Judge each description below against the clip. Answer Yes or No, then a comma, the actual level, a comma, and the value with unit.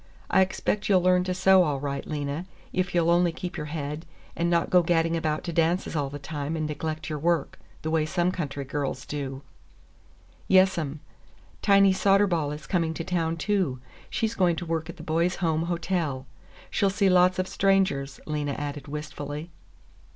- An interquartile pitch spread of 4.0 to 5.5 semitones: No, average, 3.5 semitones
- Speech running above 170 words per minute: Yes, average, 180 wpm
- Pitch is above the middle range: No, medium, 165 Hz